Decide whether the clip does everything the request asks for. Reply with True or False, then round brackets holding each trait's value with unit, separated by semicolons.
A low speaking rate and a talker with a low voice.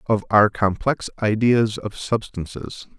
True (120 wpm; 110 Hz)